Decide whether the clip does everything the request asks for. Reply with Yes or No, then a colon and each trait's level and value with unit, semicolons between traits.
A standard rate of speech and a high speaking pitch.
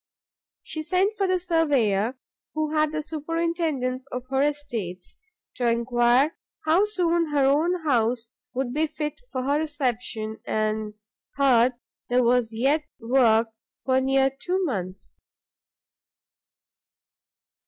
No: slow, 120 wpm; very high, 270 Hz